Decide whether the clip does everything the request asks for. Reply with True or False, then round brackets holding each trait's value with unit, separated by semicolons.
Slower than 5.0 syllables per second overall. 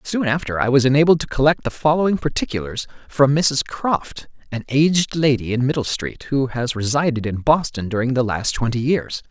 False (5.3 syllables/s)